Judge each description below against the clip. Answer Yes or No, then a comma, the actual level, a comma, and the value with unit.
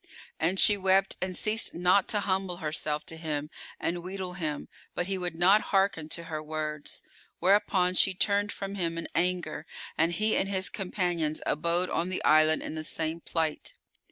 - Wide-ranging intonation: No, average, 3.2 semitones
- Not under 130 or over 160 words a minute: No, average, 180 wpm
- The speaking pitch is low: No, medium, 175 Hz